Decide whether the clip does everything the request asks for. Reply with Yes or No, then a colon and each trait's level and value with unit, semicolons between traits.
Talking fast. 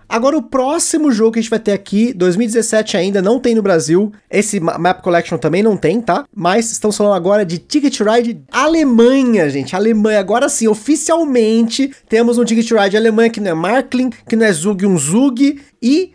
Yes: fast, 195 wpm